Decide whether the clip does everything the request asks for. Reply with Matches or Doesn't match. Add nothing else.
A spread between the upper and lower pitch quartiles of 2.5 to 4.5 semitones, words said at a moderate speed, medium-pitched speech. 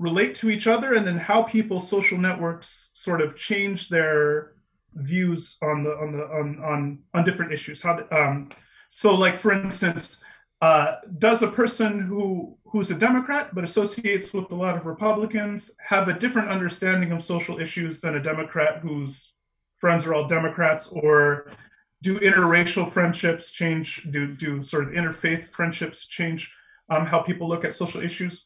Matches